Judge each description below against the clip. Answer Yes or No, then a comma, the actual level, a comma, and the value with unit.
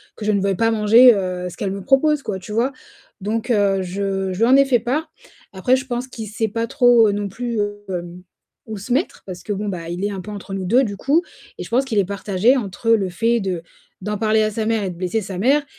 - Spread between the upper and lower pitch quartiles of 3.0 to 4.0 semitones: Yes, average, 3.7 semitones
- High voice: Yes, high, 210 Hz